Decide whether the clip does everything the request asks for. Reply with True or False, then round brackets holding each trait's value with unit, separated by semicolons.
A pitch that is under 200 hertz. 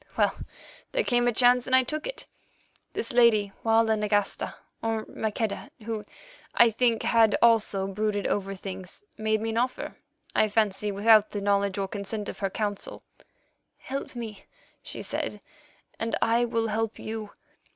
False (220 Hz)